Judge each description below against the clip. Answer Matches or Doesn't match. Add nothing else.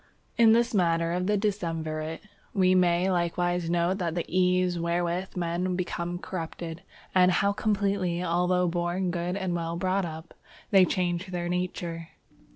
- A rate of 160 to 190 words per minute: Doesn't match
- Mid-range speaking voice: Matches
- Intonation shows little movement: Matches